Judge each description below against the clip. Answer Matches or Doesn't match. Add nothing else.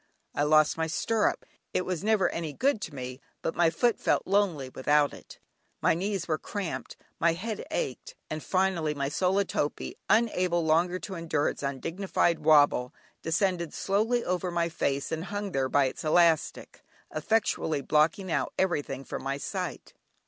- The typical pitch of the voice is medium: Matches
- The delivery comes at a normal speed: Matches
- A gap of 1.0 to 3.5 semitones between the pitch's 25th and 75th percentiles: Doesn't match